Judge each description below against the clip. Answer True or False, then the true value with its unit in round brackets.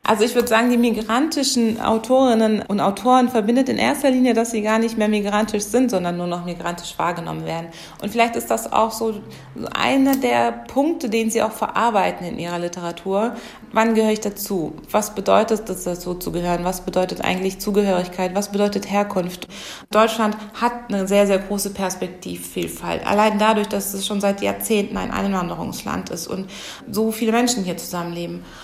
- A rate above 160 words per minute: True (170 wpm)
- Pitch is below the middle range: False (210 Hz)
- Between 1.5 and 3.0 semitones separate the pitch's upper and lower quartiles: False (3.5 semitones)